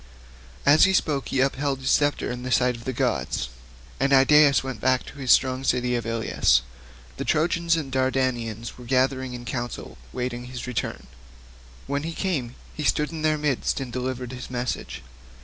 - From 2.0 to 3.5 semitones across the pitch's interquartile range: Yes, narrow, 2.4 semitones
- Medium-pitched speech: No, low, 130 Hz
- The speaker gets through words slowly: No, average, 185 wpm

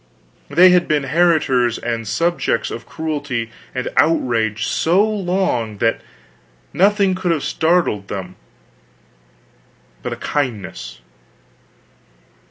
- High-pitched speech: No, medium, 145 Hz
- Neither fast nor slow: No, slow, 100 wpm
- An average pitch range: No, wide, 7.4 semitones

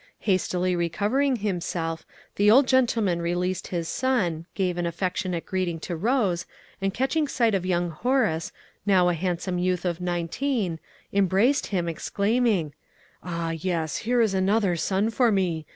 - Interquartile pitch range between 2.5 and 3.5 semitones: No, average, 4.1 semitones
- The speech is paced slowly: No, average, 145 wpm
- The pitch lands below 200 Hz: Yes, medium, 185 Hz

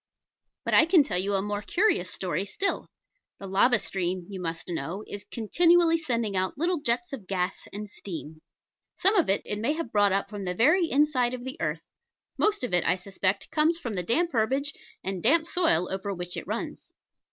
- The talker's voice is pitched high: Yes, high, 210 Hz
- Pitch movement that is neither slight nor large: No, wide, 8.0 semitones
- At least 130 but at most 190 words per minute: No, average, 200 wpm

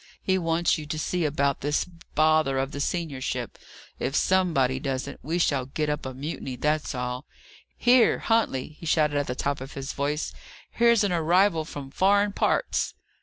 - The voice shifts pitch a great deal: No, average, 4.2 semitones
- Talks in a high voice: No, medium, 150 Hz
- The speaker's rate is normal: Yes, average, 170 wpm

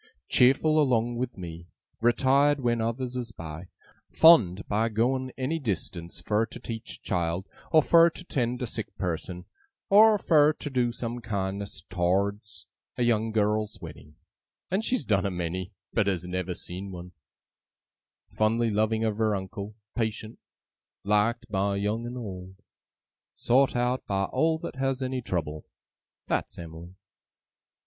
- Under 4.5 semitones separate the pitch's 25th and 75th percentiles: No, average, 4.8 semitones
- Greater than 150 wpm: No, average, 145 wpm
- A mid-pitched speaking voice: No, low, 110 Hz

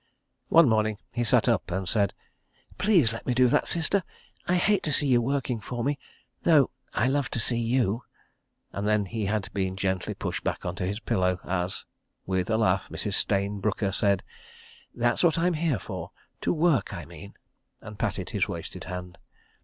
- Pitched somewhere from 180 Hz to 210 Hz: No, low, 110 Hz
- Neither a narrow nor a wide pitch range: No, wide, 5.7 semitones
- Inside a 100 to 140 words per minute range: No, average, 175 wpm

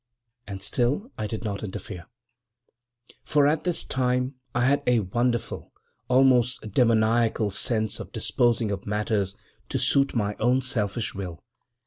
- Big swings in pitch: No, average, 3.2 semitones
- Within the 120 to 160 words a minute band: Yes, average, 150 wpm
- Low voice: Yes, low, 115 Hz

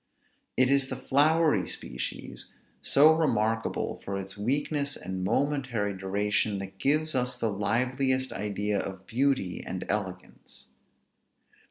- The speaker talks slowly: Yes, slow, 120 wpm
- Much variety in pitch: Yes, wide, 5.8 semitones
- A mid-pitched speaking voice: No, low, 115 Hz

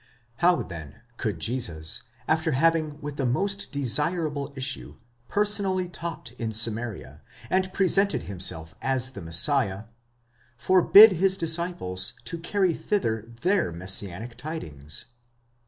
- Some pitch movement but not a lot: No, wide, 8.9 semitones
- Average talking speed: No, slow, 115 wpm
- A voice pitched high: No, medium, 140 Hz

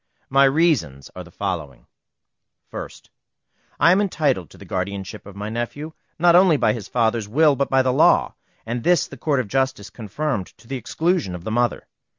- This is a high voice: No, low, 120 Hz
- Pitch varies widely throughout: Yes, wide, 6.9 semitones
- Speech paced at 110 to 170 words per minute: No, average, 180 wpm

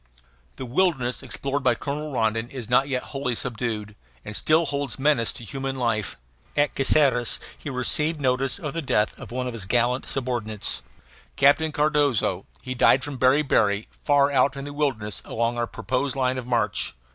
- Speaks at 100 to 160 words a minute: No, average, 170 wpm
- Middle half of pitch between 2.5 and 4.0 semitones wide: Yes, average, 3.2 semitones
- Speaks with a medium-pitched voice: No, low, 130 Hz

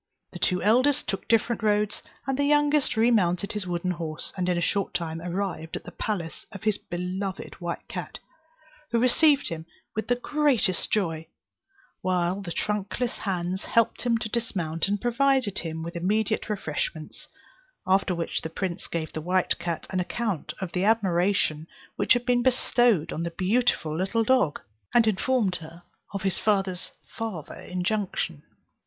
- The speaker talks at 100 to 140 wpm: No, average, 160 wpm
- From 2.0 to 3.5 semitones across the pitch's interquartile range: No, average, 4.7 semitones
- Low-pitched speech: No, high, 195 Hz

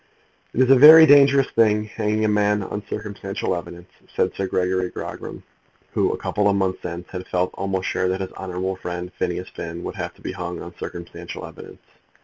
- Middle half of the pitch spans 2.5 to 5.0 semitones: Yes, average, 2.8 semitones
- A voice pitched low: Yes, very low, 95 Hz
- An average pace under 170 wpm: No, average, 195 wpm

